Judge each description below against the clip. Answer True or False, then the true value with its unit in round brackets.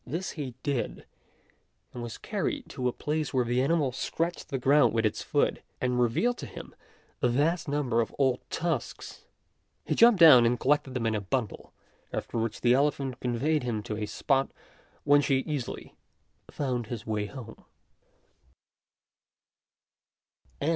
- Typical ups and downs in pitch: True (3.7 semitones)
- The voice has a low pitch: True (130 Hz)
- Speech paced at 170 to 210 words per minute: False (155 wpm)